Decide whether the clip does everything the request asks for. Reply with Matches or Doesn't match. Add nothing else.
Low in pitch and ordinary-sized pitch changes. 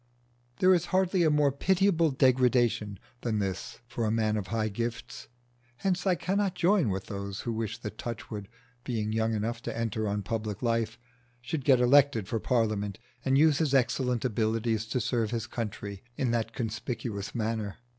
Matches